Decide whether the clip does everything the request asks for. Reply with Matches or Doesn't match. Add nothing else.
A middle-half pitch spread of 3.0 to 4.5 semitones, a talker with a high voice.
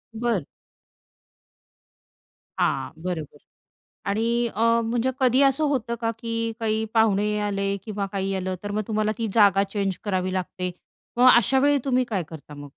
Matches